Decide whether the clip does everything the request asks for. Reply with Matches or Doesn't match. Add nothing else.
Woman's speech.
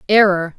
Matches